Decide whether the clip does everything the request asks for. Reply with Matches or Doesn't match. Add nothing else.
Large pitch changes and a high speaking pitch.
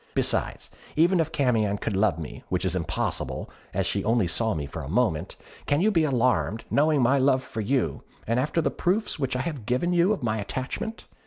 Doesn't match